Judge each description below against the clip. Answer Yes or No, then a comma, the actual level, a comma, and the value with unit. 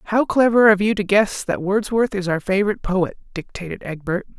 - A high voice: Yes, high, 200 Hz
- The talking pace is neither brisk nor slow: Yes, average, 190 wpm